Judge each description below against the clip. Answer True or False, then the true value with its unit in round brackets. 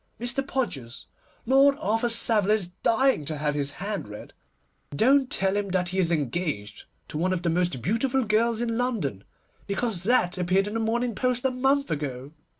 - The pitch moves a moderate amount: False (6.3 semitones)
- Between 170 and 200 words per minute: True (180 wpm)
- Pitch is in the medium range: False (205 Hz)